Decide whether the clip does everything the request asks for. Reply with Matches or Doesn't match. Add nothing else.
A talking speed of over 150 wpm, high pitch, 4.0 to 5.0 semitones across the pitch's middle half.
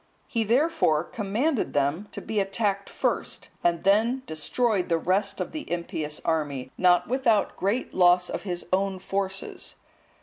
Doesn't match